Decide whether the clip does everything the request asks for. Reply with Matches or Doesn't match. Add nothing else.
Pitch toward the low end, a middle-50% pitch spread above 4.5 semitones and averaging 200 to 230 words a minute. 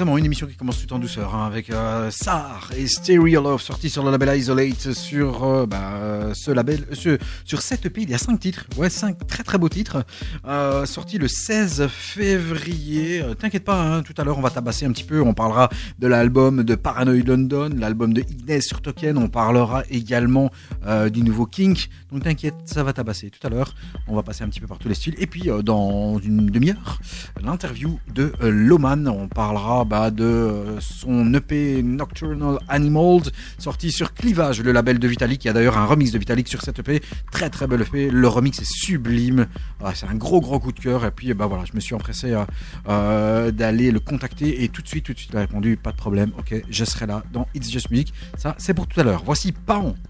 Matches